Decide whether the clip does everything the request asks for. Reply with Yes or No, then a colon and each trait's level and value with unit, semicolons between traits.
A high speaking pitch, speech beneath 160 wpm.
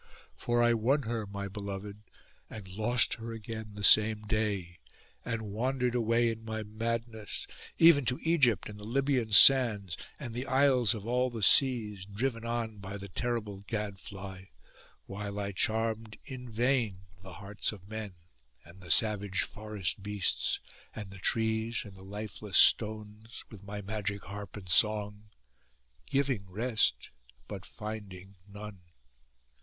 No: low, 110 Hz; average, 145 wpm